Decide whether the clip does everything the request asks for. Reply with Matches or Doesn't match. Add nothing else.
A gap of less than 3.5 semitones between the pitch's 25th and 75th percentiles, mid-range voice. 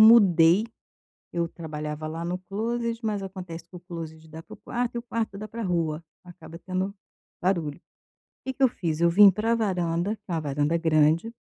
Doesn't match